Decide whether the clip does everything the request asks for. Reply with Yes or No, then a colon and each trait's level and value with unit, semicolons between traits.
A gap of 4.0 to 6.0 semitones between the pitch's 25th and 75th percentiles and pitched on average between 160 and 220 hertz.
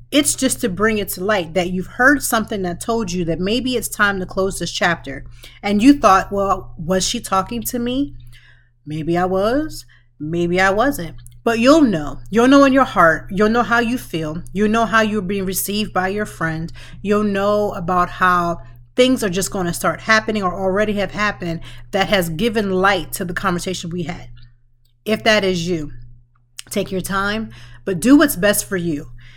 Yes: average, 4.7 semitones; high, 190 Hz